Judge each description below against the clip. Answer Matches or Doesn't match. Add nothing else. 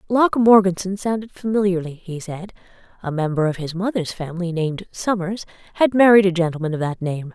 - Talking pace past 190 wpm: Doesn't match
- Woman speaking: Matches